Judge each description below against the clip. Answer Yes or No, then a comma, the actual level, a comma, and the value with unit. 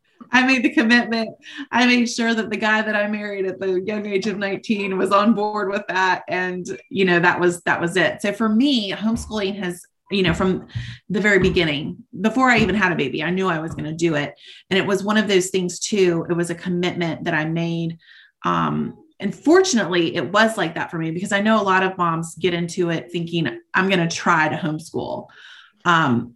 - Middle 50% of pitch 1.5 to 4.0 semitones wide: Yes, average, 3.7 semitones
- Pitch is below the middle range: No, high, 190 Hz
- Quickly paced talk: Yes, fast, 225 wpm